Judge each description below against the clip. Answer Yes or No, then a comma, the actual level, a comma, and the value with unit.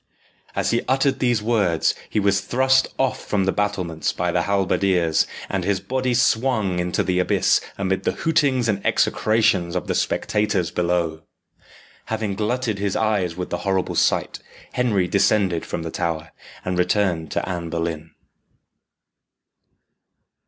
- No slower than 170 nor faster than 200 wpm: No, average, 145 wpm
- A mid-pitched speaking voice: No, low, 100 Hz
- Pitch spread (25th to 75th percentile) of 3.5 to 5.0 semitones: Yes, average, 3.8 semitones